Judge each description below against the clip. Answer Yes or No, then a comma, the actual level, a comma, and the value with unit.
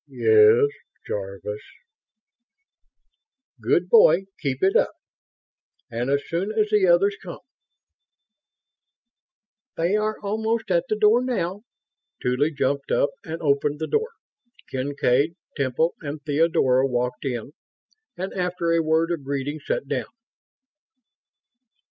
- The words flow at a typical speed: No, slow, 120 wpm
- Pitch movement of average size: No, wide, 7.2 semitones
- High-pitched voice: No, medium, 165 Hz